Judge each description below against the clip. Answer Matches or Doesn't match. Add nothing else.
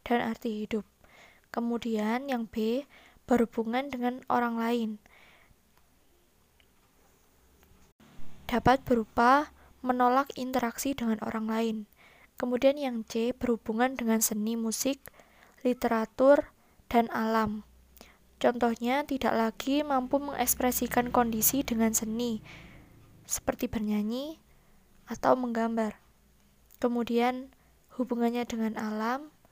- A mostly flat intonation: Matches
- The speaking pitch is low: Doesn't match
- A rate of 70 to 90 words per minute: Matches